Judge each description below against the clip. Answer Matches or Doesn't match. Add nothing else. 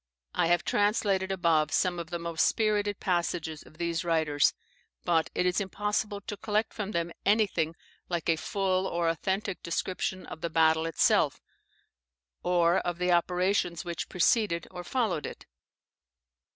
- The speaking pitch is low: Doesn't match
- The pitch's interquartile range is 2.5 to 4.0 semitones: Matches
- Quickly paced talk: Doesn't match